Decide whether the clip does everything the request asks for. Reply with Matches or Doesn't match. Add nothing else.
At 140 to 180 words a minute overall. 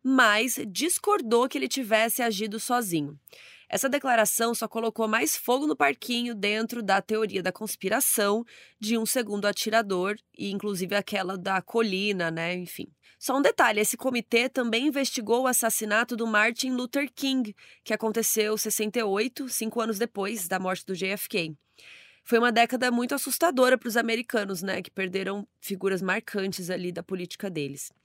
Matches